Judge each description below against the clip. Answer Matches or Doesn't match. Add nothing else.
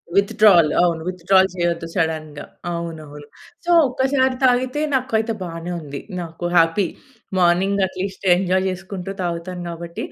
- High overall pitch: Doesn't match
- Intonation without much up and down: Doesn't match